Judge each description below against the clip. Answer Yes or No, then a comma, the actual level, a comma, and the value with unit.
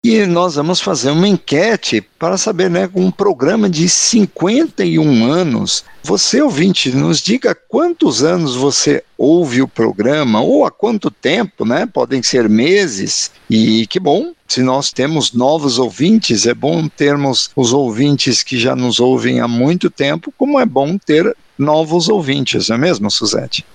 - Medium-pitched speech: Yes, medium, 150 Hz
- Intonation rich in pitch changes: Yes, wide, 6.1 semitones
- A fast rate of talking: No, average, 160 wpm